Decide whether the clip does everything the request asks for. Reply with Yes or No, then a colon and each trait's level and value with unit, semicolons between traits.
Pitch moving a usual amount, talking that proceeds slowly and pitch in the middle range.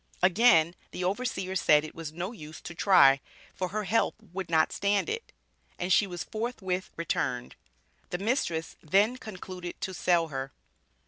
No: average, 3.7 semitones; average, 155 wpm; medium, 180 Hz